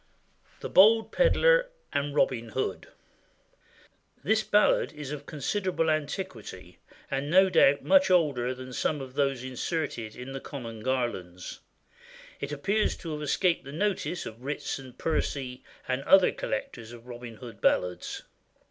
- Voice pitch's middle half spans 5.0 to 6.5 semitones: Yes, wide, 5.5 semitones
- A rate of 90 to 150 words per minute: Yes, average, 140 wpm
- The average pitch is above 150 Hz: No, medium, 140 Hz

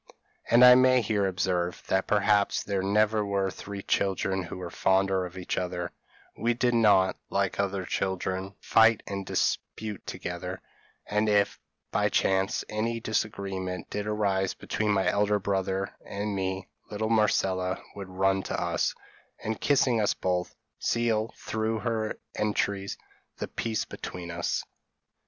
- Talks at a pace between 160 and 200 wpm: No, average, 140 wpm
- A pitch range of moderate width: No, narrow, 2.2 semitones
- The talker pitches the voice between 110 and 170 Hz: No, low, 100 Hz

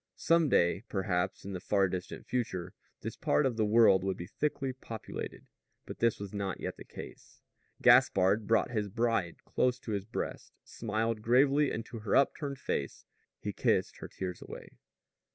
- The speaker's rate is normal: Yes, average, 170 wpm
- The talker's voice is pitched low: Yes, low, 110 Hz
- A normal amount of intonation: Yes, average, 4.0 semitones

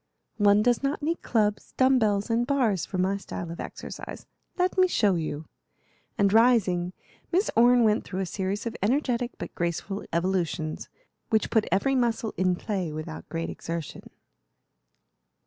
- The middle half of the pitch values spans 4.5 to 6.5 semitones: Yes, average, 5.0 semitones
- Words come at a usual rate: Yes, average, 155 wpm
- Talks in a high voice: Yes, high, 205 Hz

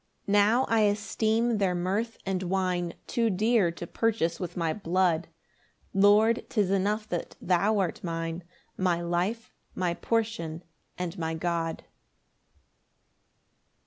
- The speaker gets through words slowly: Yes, slow, 125 wpm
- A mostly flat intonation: No, average, 3.8 semitones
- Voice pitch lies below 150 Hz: No, high, 190 Hz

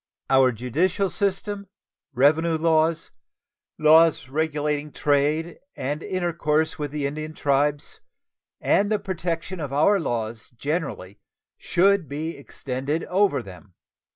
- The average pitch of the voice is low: No, medium, 155 Hz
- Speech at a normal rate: No, slow, 110 wpm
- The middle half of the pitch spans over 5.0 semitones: No, average, 3.3 semitones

